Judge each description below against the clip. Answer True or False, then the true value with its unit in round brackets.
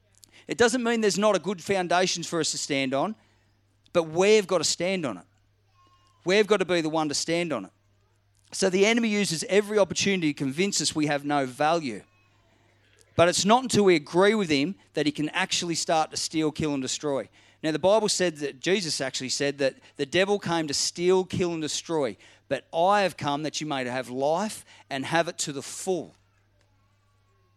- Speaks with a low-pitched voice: False (155 Hz)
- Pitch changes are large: True (7.6 semitones)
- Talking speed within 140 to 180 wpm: False (200 wpm)